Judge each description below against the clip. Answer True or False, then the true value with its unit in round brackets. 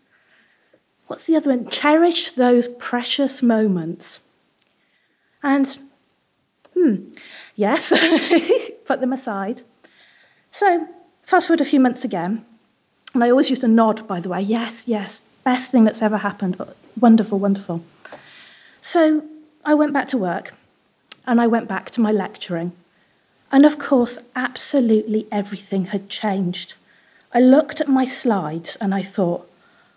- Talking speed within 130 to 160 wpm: True (135 wpm)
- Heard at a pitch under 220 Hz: False (245 Hz)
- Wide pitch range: True (5.8 semitones)